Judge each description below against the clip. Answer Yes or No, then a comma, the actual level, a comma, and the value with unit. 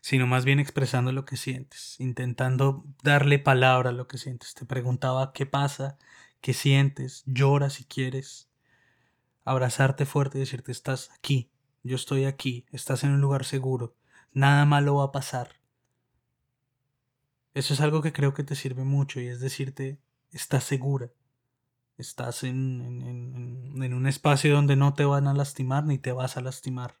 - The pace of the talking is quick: No, average, 165 wpm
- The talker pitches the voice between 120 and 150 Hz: Yes, low, 135 Hz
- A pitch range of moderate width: No, narrow, 1.5 semitones